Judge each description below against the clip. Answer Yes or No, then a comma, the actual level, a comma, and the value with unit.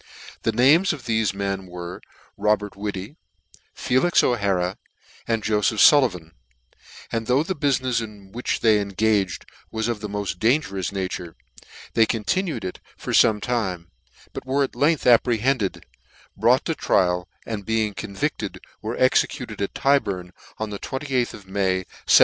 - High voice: No, low, 110 Hz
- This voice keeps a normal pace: Yes, average, 150 wpm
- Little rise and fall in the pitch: No, average, 4.2 semitones